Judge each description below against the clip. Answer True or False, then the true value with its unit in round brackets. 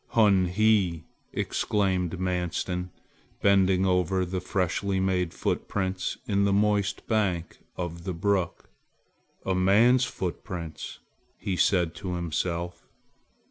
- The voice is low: True (95 Hz)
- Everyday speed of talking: False (105 wpm)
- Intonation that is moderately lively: False (2.0 semitones)